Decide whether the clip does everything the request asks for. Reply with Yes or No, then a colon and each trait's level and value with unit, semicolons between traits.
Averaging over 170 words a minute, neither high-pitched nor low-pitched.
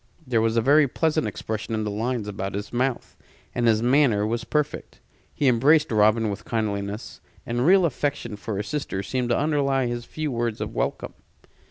No: average, 185 wpm; low, 120 Hz